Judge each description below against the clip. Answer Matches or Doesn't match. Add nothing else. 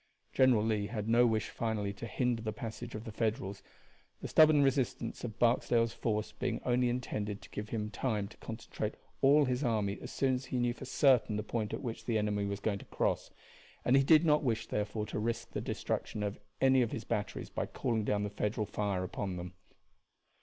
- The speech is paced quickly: Matches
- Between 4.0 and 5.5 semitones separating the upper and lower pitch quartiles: Doesn't match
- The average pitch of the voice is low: Matches